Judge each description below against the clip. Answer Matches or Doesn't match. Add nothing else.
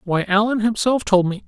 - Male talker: Matches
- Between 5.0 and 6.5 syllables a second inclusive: Matches